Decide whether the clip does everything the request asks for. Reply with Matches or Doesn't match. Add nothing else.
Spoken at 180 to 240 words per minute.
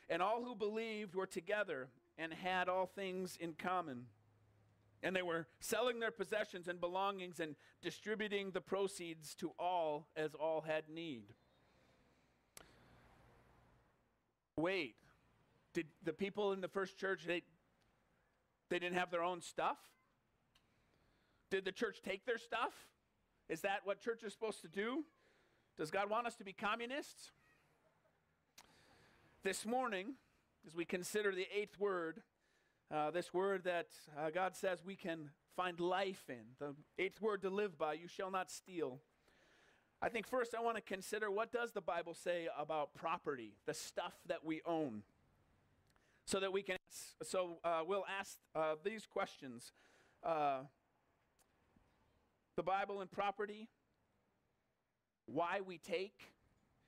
Doesn't match